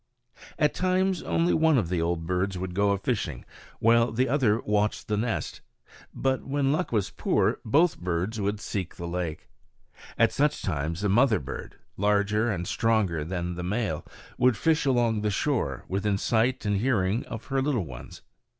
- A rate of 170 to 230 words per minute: Yes, average, 175 wpm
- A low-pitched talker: Yes, low, 105 Hz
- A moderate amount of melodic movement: No, wide, 5.8 semitones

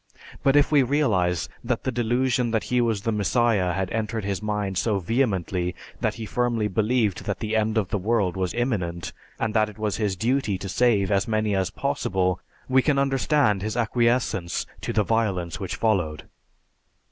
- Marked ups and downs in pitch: No, average, 3.8 semitones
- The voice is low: Yes, low, 110 Hz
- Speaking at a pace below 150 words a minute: No, average, 180 wpm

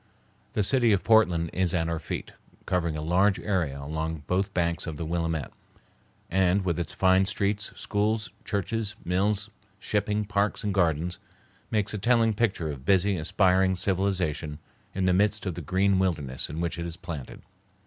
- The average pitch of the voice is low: Yes, very low, 95 Hz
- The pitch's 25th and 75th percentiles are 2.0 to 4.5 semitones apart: Yes, average, 3.5 semitones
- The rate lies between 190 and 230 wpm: No, average, 170 wpm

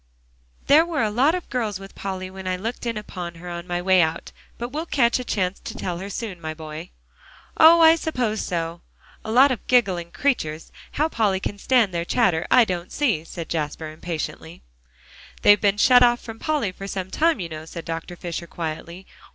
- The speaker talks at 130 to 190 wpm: No, average, 200 wpm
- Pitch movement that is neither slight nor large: No, wide, 6.0 semitones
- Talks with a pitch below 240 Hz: Yes, high, 190 Hz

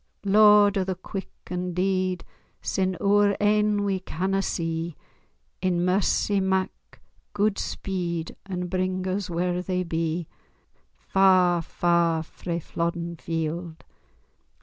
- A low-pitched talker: No, medium, 185 Hz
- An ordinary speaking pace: No, slow, 115 wpm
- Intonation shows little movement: Yes, narrow, 2.2 semitones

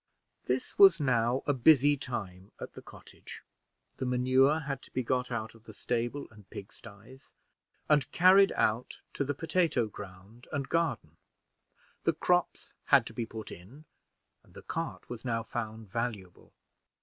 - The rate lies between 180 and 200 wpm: No, average, 155 wpm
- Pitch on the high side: No, low, 125 Hz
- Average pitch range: Yes, average, 4.4 semitones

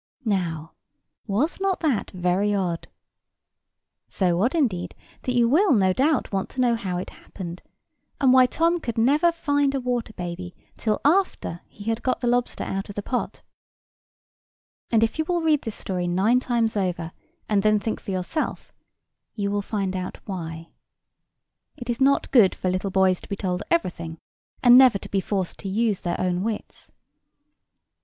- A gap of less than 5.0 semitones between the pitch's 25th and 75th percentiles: No, wide, 5.5 semitones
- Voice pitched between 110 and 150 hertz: No, high, 210 Hz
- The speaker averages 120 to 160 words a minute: No, average, 175 wpm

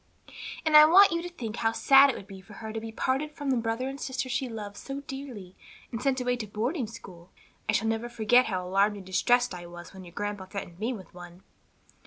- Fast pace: Yes, fast, 245 wpm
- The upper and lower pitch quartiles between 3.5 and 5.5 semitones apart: Yes, average, 4.9 semitones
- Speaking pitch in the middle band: No, high, 225 Hz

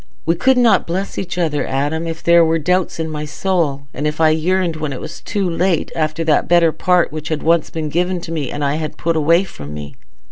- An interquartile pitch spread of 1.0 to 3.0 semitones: Yes, narrow, 2.4 semitones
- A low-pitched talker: No, medium, 165 Hz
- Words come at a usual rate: No, fast, 235 wpm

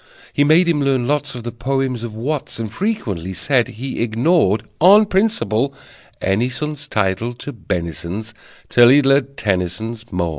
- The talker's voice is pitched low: Yes, low, 120 Hz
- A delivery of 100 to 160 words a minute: Yes, average, 155 wpm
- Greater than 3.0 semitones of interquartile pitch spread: Yes, average, 5.1 semitones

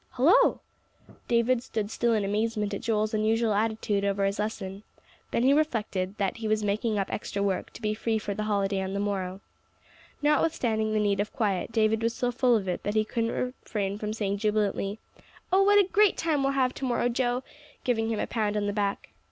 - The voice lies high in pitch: Yes, high, 215 Hz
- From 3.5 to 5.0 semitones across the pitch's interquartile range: No, average, 2.8 semitones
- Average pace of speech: No, fast, 210 wpm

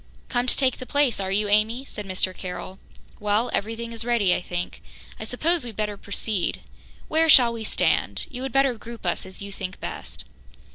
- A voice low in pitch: No, high, 220 Hz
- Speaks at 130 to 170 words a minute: No, average, 195 wpm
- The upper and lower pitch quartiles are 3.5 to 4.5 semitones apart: Yes, average, 3.9 semitones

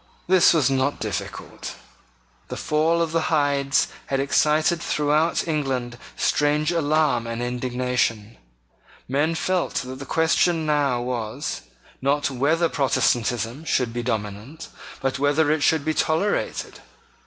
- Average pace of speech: No, slow, 125 wpm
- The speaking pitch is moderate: Yes, medium, 145 Hz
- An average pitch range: Yes, average, 3.9 semitones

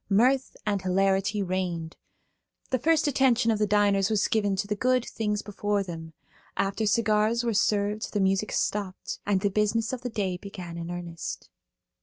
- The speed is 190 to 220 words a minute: No, average, 170 wpm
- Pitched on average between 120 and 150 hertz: No, high, 205 Hz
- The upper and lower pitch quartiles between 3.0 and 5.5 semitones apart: No, narrow, 2.5 semitones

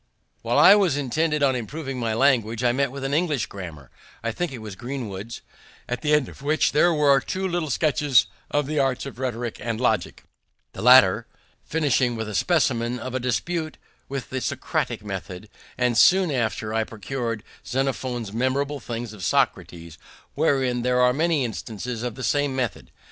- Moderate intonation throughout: Yes, average, 3.8 semitones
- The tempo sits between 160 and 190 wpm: Yes, average, 175 wpm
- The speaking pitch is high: No, low, 125 Hz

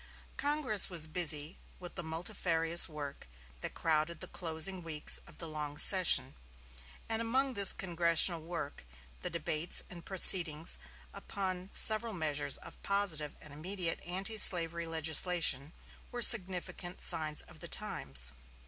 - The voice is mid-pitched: Yes, medium, 170 Hz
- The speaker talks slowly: Yes, slow, 130 wpm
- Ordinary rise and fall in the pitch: Yes, average, 3.4 semitones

